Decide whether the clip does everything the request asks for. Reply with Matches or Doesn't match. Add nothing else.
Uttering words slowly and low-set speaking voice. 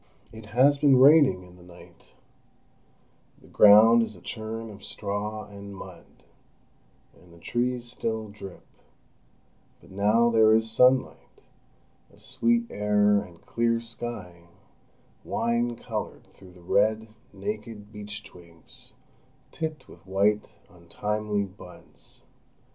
Matches